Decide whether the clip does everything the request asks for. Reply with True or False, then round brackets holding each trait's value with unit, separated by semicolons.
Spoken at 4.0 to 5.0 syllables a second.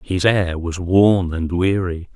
False (3.5 syllables/s)